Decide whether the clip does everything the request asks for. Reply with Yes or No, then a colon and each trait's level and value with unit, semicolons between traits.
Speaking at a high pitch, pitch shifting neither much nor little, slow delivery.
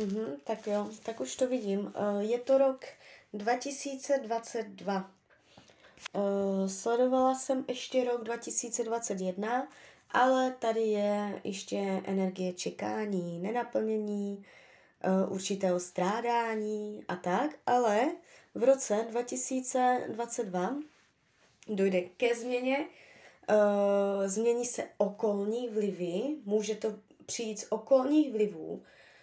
Yes: high, 220 Hz; average, 3.6 semitones; slow, 90 wpm